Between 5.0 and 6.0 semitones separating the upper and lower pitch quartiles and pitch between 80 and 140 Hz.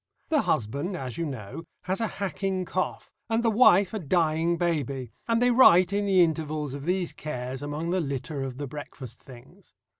No: average, 5.3 semitones; medium, 165 Hz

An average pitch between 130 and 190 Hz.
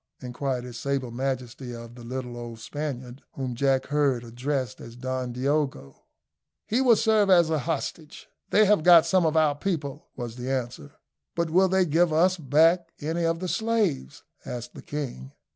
Yes: medium, 140 Hz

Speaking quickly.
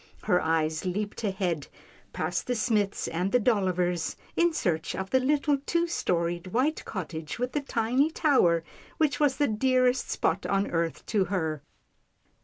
No: average, 155 wpm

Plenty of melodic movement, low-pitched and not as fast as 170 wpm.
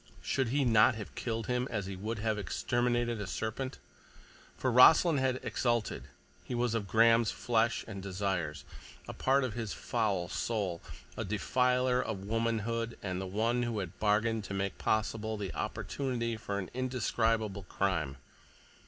No: average, 3.1 semitones; low, 110 Hz; average, 155 wpm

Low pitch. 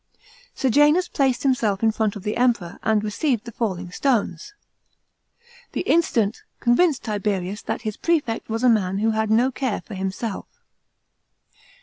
No: high, 225 Hz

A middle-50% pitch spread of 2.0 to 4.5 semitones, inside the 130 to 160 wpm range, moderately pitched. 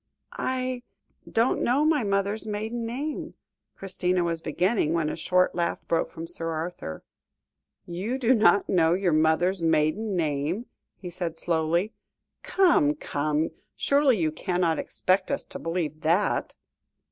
No: average, 5.3 semitones; average, 140 wpm; medium, 180 Hz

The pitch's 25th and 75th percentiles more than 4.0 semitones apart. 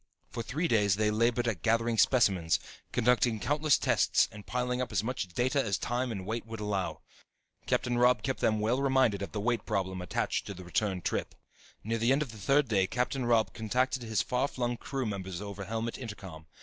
No: average, 3.5 semitones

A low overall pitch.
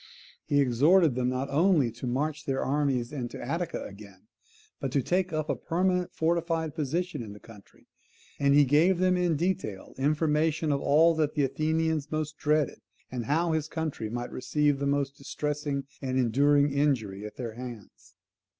No: medium, 145 Hz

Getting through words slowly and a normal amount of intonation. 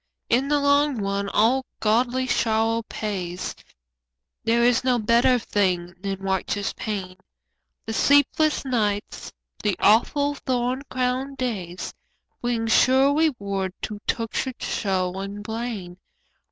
Yes: slow, 115 wpm; average, 4.4 semitones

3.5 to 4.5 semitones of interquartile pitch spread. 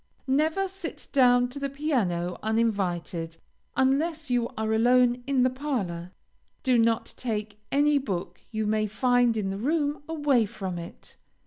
No: average, 5.1 semitones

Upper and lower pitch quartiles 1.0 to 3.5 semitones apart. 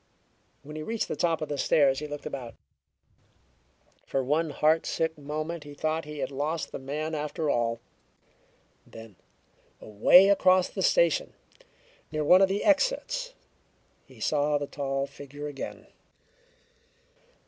Yes: average, 2.8 semitones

